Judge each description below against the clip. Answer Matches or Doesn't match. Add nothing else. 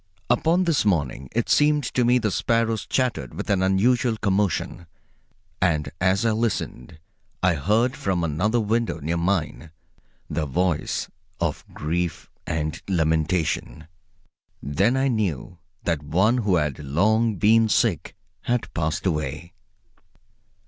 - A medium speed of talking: Doesn't match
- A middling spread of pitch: Doesn't match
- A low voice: Matches